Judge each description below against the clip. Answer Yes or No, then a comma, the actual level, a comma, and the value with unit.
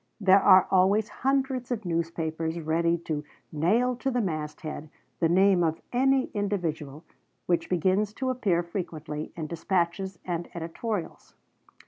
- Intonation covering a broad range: No, average, 4.3 semitones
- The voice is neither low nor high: Yes, medium, 175 Hz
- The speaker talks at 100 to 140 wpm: Yes, slow, 135 wpm